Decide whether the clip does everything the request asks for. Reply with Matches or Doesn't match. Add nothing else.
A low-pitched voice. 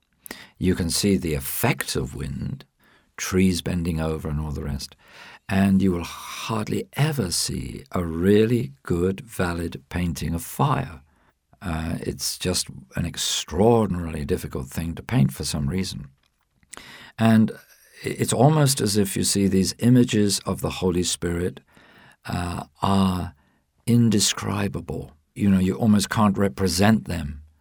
Matches